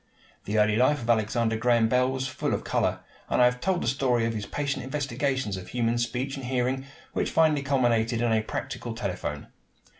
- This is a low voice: Yes, low, 120 Hz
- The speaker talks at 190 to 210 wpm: Yes, average, 200 wpm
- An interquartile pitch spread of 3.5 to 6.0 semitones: No, average, 2.8 semitones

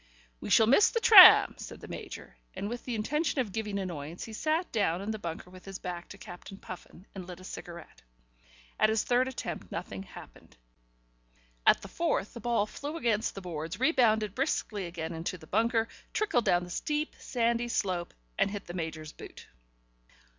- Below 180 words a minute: No, average, 185 wpm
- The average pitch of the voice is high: Yes, high, 205 Hz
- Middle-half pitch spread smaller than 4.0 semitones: No, average, 5.2 semitones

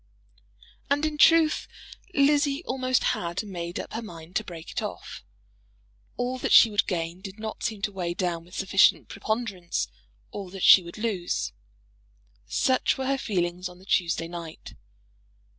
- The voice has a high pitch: Yes, high, 195 Hz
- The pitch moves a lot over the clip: Yes, wide, 5.9 semitones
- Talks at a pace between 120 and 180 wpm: Yes, average, 160 wpm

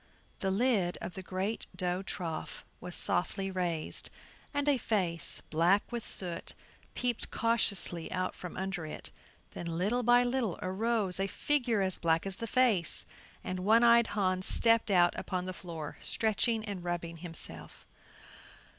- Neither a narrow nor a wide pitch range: Yes, average, 4.4 semitones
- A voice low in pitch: No, high, 190 Hz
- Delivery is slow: No, average, 150 wpm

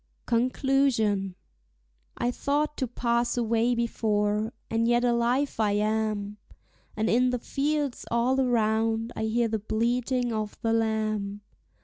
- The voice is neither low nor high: No, high, 230 Hz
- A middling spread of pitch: No, narrow, 2.3 semitones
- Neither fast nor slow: No, slow, 125 wpm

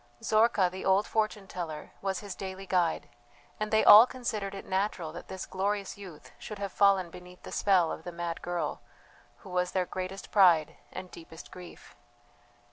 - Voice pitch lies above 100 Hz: Yes, high, 190 Hz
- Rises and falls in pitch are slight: Yes, narrow, 2.2 semitones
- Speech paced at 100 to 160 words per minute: No, average, 175 wpm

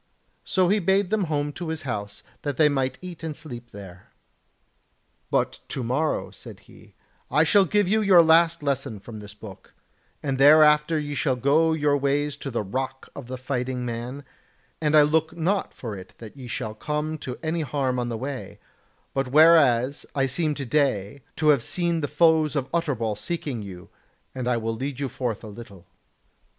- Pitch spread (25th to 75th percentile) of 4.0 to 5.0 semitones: Yes, average, 4.4 semitones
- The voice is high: No, medium, 140 Hz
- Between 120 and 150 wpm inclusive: No, average, 185 wpm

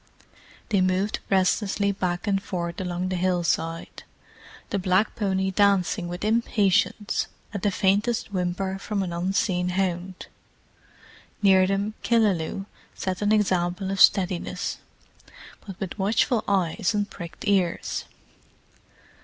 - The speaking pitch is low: No, high, 190 Hz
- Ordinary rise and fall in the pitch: No, narrow, 2.0 semitones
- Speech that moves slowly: Yes, slow, 115 wpm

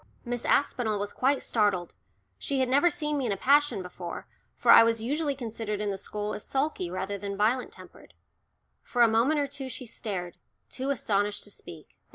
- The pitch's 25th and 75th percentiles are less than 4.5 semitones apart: No, average, 4.8 semitones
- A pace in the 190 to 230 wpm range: Yes, average, 195 wpm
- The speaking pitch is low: No, high, 230 Hz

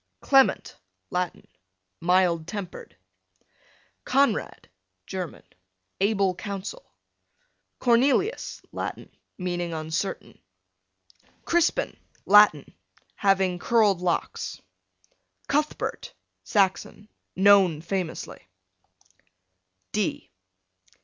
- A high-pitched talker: Yes, high, 195 Hz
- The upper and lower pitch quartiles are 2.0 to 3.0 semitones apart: No, average, 3.7 semitones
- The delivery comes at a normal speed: No, slow, 60 wpm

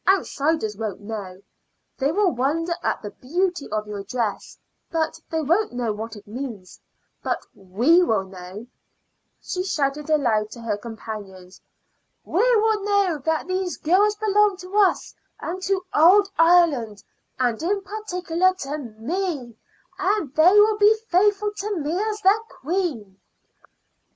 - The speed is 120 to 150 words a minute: Yes, average, 140 wpm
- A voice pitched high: Yes, very high, 320 Hz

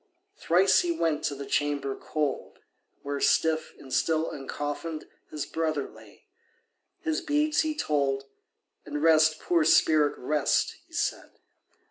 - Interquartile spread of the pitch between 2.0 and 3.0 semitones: Yes, narrow, 2.4 semitones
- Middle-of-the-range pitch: Yes, medium, 155 Hz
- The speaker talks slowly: Yes, slow, 130 wpm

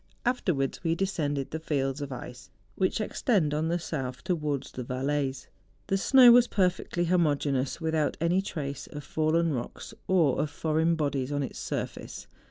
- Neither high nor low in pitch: Yes, medium, 155 Hz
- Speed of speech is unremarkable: Yes, average, 160 wpm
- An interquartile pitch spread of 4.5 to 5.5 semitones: No, average, 3.8 semitones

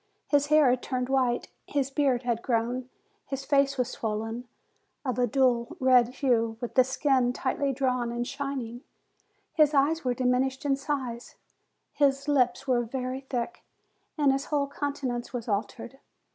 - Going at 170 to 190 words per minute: No, average, 160 wpm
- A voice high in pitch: Yes, very high, 255 Hz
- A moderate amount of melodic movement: No, narrow, 2.3 semitones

